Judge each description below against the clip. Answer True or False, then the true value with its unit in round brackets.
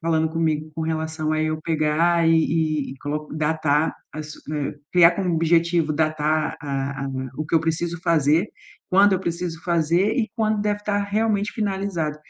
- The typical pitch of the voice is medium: True (160 Hz)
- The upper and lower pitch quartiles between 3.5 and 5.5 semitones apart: False (2.6 semitones)